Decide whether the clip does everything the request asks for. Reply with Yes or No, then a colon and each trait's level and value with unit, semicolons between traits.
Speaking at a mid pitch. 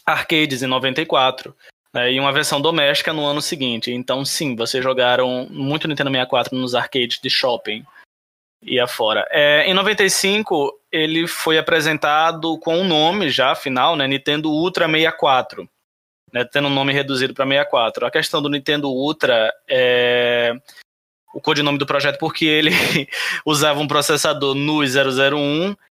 Yes: medium, 145 Hz